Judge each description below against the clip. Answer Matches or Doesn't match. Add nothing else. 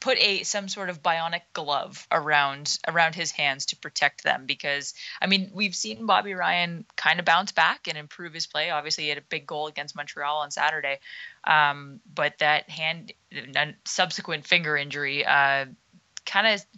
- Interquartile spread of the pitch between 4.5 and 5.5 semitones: Doesn't match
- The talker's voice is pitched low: Doesn't match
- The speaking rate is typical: Matches